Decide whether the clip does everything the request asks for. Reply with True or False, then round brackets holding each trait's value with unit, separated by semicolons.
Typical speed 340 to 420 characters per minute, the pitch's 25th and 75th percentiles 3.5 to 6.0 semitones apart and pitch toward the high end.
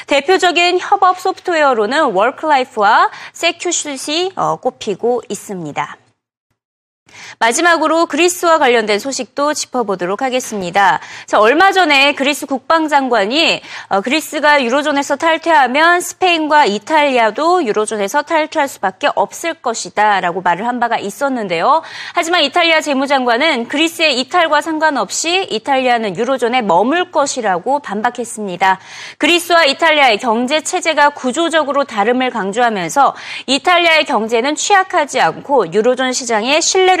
True (345 characters per minute; 5.7 semitones; 285 Hz)